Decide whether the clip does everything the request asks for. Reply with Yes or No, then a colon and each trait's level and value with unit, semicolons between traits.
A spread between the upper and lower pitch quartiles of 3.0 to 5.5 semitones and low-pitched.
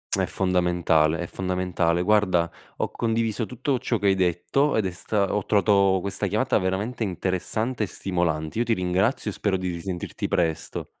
Yes: average, 3.4 semitones; very low, 95 Hz